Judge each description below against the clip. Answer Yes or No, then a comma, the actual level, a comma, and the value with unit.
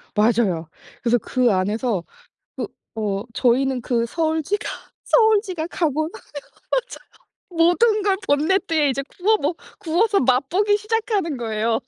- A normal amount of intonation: No, wide, 8.7 semitones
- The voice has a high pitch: Yes, very high, 310 Hz